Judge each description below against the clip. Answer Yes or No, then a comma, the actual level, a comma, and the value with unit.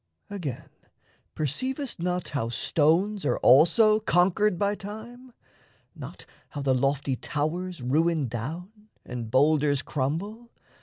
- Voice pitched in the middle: Yes, medium, 165 Hz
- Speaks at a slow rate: Yes, slow, 110 wpm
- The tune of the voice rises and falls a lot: Yes, wide, 6.6 semitones